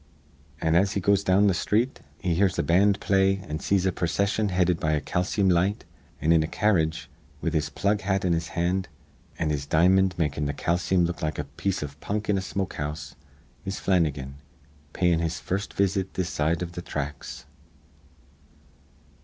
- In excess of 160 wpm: Yes, average, 180 wpm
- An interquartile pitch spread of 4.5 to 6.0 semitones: No, average, 3.6 semitones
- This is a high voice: No, very low, 90 Hz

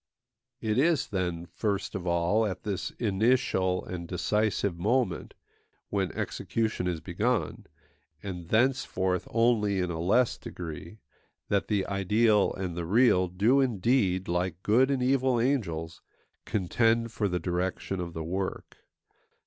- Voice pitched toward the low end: Yes, low, 100 Hz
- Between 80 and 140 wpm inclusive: Yes, slow, 135 wpm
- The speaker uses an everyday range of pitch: Yes, average, 4.3 semitones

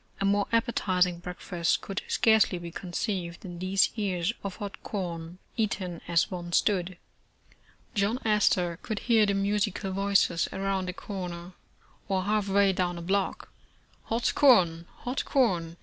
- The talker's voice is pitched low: No, high, 190 Hz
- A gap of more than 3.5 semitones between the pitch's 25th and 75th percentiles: No, narrow, 2.6 semitones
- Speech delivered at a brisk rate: No, average, 150 wpm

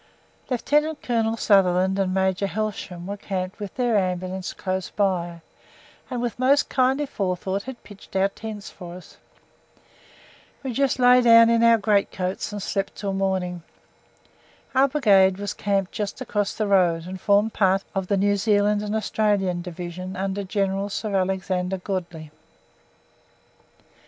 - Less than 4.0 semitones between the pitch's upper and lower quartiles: Yes, average, 2.7 semitones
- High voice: Yes, high, 195 Hz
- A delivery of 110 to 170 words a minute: Yes, average, 145 wpm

